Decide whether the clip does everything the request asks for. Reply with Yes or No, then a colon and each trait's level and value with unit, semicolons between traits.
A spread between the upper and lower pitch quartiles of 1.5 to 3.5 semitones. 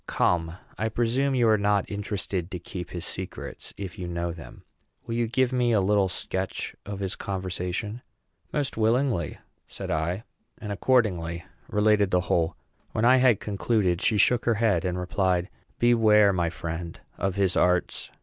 No: average, 4.0 semitones